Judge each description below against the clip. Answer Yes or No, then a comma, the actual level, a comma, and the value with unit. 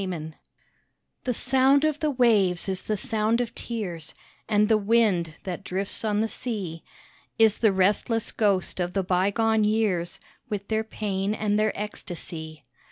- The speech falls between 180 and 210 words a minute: No, average, 160 wpm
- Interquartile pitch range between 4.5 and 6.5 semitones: No, average, 3.2 semitones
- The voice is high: Yes, high, 210 Hz